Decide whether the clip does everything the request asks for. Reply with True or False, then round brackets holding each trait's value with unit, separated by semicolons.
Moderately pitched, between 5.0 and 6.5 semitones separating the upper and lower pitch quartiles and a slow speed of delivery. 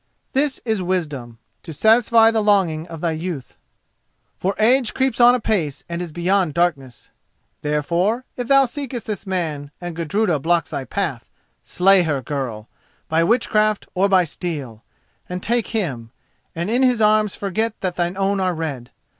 False (180 Hz; 5.5 semitones; 155 wpm)